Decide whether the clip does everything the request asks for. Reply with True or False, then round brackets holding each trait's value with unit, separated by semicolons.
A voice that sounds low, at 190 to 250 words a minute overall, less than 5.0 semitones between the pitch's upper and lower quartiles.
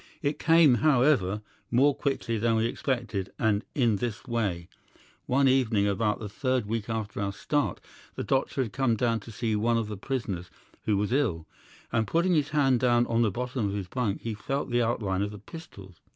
True (115 Hz; 195 wpm; 4.1 semitones)